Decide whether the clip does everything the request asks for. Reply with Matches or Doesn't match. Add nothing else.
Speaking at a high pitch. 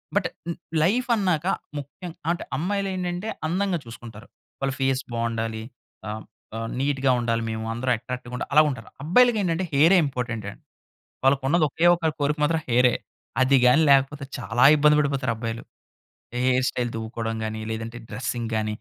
Doesn't match